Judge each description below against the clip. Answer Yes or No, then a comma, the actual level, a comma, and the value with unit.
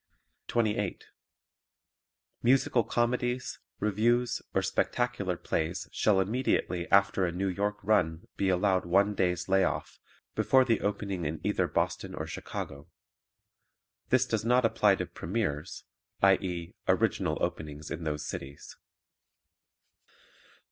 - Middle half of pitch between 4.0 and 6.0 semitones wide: Yes, average, 4.6 semitones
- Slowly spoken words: Yes, slow, 115 wpm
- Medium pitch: No, low, 100 Hz